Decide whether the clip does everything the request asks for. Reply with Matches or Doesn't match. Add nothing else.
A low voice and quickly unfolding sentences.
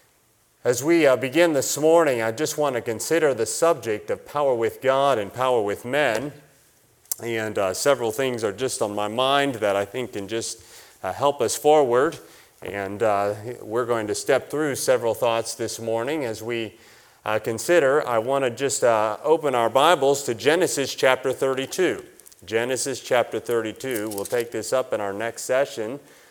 Doesn't match